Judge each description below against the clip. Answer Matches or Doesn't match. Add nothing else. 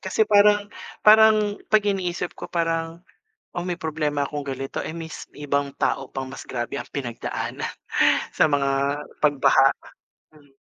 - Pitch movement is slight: Doesn't match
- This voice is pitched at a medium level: Matches